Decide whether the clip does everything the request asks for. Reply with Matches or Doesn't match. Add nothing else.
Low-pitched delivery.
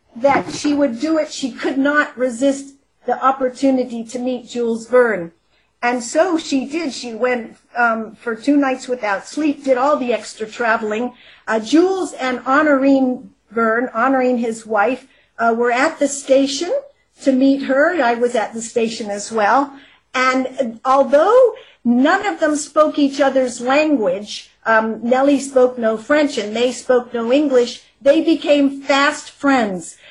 Doesn't match